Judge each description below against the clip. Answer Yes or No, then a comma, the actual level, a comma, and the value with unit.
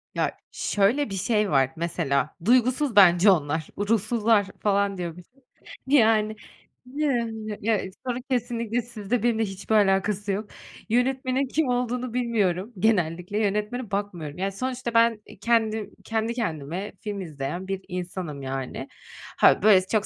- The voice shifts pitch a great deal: No, average, 4.0 semitones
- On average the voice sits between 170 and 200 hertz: No, high, 210 Hz